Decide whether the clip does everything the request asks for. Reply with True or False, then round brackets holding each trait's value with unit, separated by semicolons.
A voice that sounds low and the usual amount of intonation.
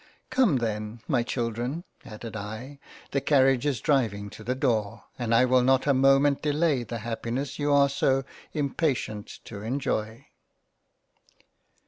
True (130 Hz; 3.7 semitones)